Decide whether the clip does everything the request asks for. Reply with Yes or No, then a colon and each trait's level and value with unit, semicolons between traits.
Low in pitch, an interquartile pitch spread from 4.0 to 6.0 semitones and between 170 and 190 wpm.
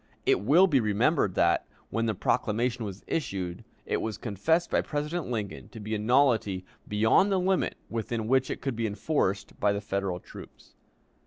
Yes: low, 110 Hz; average, 5.2 semitones; average, 175 wpm